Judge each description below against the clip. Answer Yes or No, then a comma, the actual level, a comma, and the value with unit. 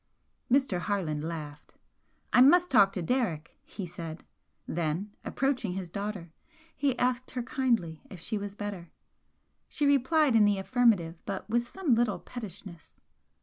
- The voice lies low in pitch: No, high, 205 Hz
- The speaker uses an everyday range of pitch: No, wide, 6.4 semitones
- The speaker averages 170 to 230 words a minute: No, average, 145 wpm